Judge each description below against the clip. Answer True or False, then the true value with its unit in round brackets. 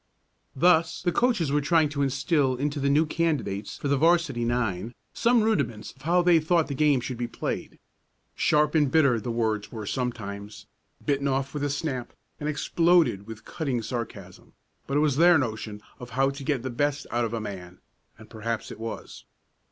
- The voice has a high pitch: False (135 Hz)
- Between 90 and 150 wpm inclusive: False (190 wpm)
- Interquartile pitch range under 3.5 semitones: False (5.1 semitones)